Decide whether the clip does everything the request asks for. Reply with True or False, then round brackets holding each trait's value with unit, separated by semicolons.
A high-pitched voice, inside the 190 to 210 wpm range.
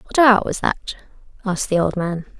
True (200 Hz; 200 wpm)